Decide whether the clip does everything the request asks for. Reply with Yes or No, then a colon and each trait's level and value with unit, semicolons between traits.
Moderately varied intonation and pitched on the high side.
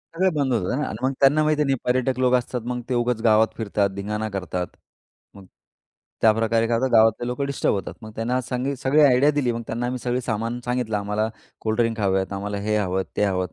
No: average, 3.2 semitones; low, 115 Hz